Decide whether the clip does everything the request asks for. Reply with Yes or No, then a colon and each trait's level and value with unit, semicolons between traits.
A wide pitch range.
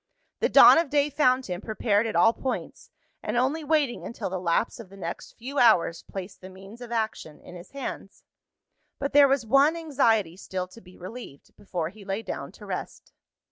Yes: wide, 6.3 semitones